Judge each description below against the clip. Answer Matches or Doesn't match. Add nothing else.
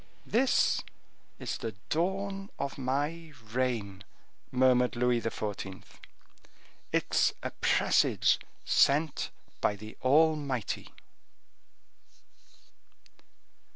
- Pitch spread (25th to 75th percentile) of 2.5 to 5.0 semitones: Doesn't match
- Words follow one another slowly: Matches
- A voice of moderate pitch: Doesn't match